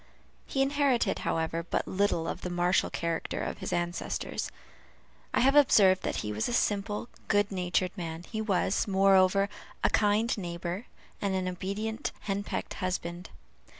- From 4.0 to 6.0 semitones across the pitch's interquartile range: No, average, 3.0 semitones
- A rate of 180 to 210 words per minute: No, average, 150 wpm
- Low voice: No, high, 190 Hz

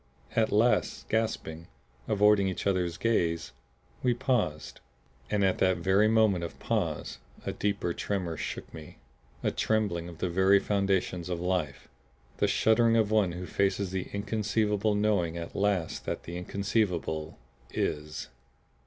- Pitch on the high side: No, very low, 95 Hz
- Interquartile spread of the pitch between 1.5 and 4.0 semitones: Yes, average, 3.5 semitones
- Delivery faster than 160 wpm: No, average, 140 wpm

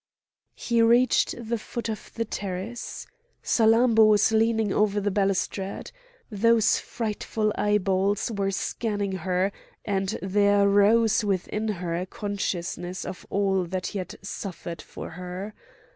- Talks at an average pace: No, slow, 130 wpm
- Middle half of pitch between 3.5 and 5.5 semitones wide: No, narrow, 2.5 semitones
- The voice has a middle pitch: No, high, 205 Hz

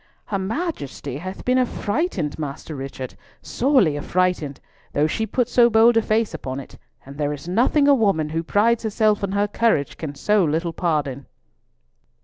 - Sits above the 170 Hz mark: Yes, medium, 185 Hz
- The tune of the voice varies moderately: No, wide, 7.2 semitones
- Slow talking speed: No, average, 165 wpm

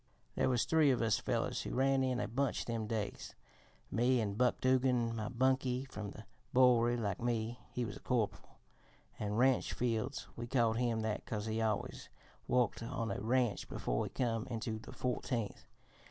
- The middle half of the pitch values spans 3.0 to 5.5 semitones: No, narrow, 2.4 semitones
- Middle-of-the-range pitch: No, low, 120 Hz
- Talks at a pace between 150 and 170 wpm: No, average, 180 wpm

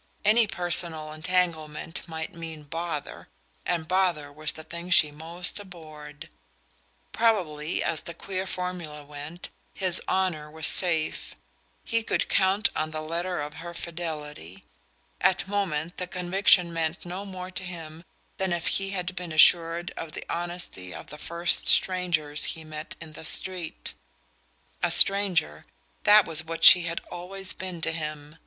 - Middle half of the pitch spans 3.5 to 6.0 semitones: No, average, 2.7 semitones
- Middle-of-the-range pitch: Yes, medium, 170 Hz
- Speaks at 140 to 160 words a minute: Yes, average, 150 wpm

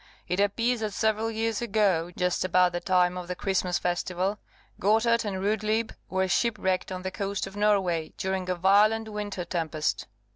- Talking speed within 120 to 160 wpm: No, average, 170 wpm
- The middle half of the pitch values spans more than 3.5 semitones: No, average, 3.0 semitones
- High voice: Yes, high, 195 Hz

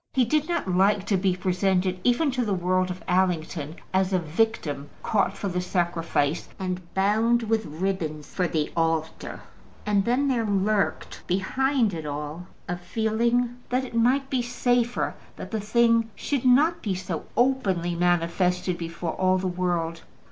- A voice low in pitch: No, high, 190 Hz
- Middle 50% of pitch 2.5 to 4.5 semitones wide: No, average, 4.9 semitones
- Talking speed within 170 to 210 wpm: No, average, 160 wpm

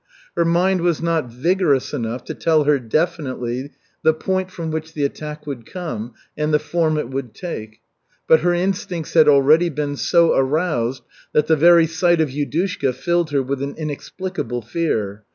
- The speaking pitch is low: No, medium, 155 Hz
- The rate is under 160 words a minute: No, average, 170 wpm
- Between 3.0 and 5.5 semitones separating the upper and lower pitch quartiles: Yes, average, 4.1 semitones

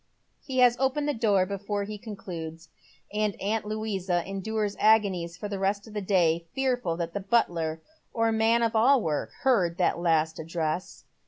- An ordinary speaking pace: Yes, average, 170 wpm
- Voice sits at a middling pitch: No, high, 200 Hz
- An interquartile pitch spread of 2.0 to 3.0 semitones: No, average, 4.4 semitones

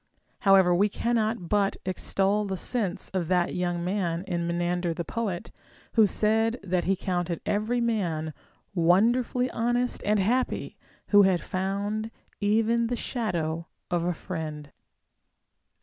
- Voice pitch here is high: Yes, high, 195 Hz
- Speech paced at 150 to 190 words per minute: No, slow, 135 wpm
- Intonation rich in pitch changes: No, average, 4.0 semitones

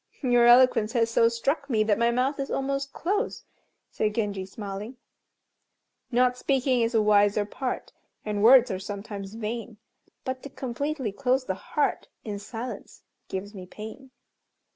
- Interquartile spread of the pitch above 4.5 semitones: No, average, 3.7 semitones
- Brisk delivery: No, average, 150 wpm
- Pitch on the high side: Yes, high, 235 Hz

